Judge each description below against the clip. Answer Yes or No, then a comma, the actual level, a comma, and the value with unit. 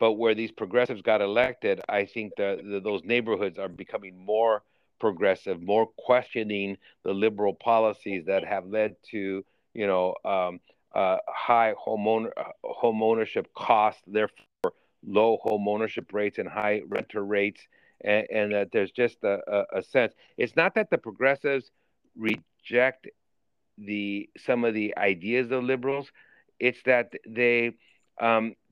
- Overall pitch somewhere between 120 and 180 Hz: No, low, 110 Hz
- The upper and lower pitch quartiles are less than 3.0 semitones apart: Yes, narrow, 2.6 semitones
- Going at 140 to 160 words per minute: Yes, average, 145 wpm